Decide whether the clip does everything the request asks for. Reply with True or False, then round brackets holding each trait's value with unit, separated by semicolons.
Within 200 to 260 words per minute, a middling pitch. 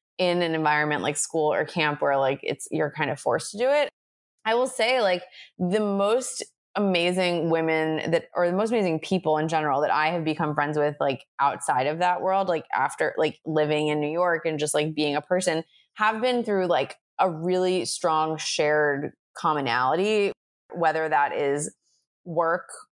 False (185 wpm; 160 Hz)